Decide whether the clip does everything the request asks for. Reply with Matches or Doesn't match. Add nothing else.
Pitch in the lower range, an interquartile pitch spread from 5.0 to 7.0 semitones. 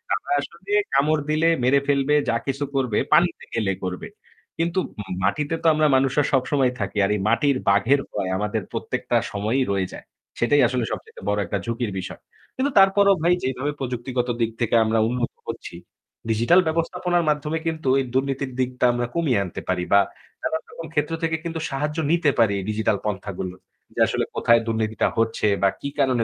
Matches